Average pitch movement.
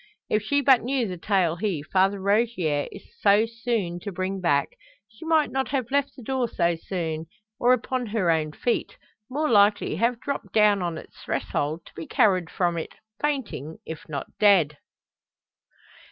No: wide, 6.1 semitones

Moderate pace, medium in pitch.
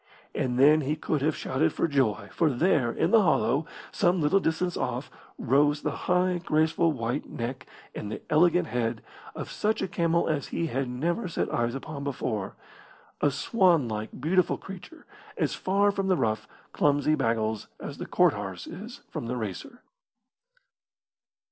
Yes: average, 160 wpm; medium, 150 Hz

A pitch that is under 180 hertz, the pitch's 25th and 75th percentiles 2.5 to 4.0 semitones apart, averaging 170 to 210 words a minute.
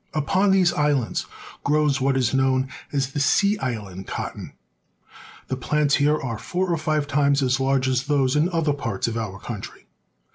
Yes: medium, 140 Hz; average, 2.8 semitones; average, 175 wpm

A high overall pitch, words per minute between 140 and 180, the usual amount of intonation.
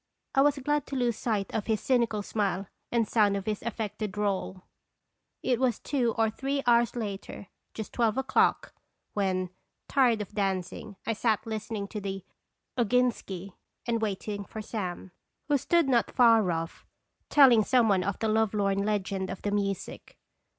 Yes: high, 215 Hz; average, 165 wpm; average, 3.2 semitones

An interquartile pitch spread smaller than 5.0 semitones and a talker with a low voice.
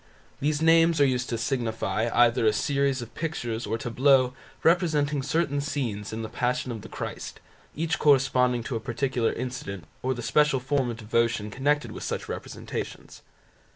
Yes: average, 3.8 semitones; low, 125 Hz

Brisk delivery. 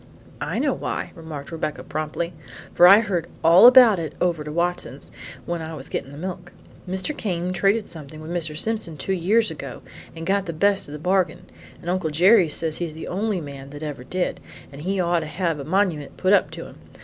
Yes: fast, 210 wpm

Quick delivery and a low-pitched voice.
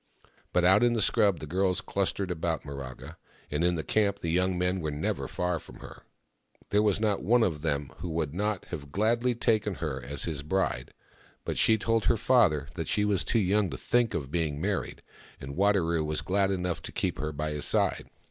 Yes: fast, 210 wpm; very low, 90 Hz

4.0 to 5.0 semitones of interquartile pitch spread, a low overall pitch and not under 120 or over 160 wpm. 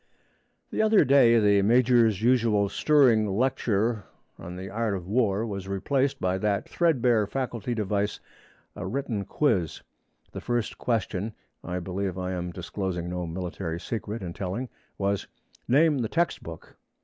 Yes: average, 4.3 semitones; low, 105 Hz; average, 140 wpm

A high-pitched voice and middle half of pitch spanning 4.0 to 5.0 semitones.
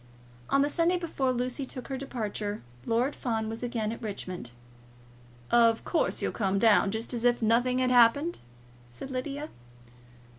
No: high, 245 Hz; average, 3.3 semitones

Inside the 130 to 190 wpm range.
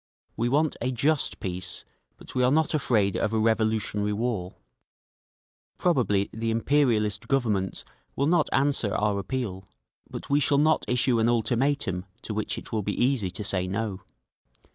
Yes: average, 155 wpm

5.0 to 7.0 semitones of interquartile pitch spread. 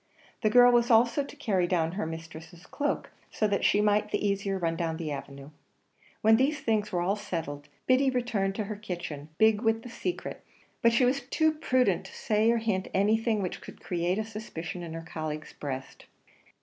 Yes: wide, 5.4 semitones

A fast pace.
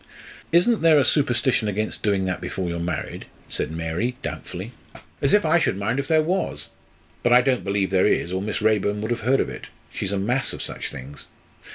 Yes: fast, 210 wpm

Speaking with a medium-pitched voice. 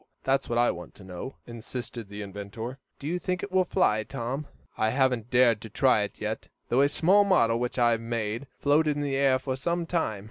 No: low, 125 Hz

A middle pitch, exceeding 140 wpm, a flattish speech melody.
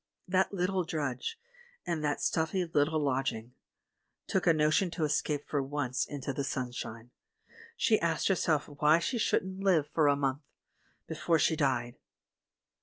No: medium, 150 Hz; average, 150 wpm; average, 3.7 semitones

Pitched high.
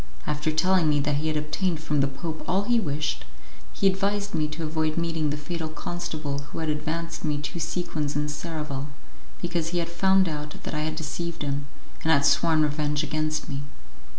No: medium, 155 Hz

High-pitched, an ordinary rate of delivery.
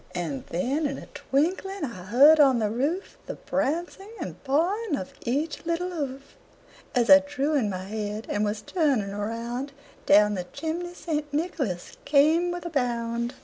Yes: very high, 275 Hz; average, 165 wpm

